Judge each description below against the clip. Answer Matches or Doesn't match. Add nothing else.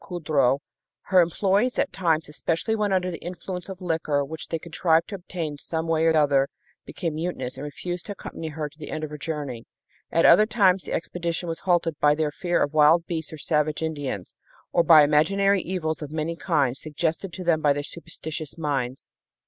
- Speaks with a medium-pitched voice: Matches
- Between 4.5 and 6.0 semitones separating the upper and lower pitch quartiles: Doesn't match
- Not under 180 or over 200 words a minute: Matches